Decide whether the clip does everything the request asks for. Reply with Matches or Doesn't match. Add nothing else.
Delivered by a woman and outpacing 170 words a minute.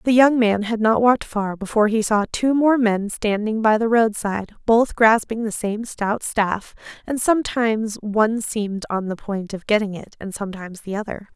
Matches